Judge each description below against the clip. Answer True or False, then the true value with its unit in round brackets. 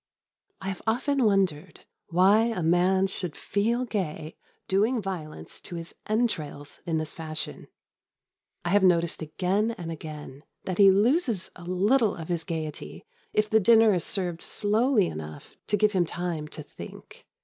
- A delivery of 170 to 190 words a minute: False (155 wpm)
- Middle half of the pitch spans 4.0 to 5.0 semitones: True (4.5 semitones)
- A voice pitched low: False (185 Hz)